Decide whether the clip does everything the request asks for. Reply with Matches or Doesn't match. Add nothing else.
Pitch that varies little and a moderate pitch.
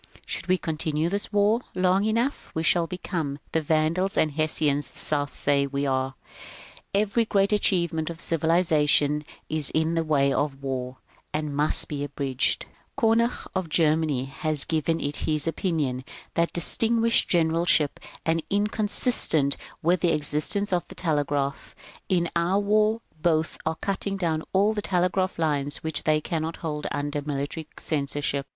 Doesn't match